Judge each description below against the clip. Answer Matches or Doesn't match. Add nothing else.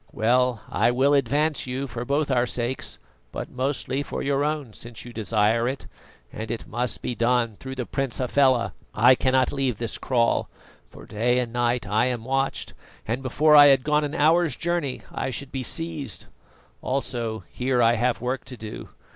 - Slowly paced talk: Doesn't match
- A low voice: Matches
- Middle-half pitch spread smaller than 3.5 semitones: Matches